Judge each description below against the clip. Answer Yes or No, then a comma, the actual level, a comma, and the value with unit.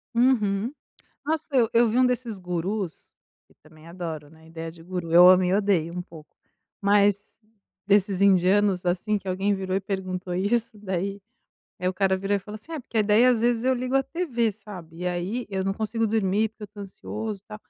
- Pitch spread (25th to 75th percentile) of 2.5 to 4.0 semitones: Yes, average, 3.4 semitones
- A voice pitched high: Yes, high, 200 Hz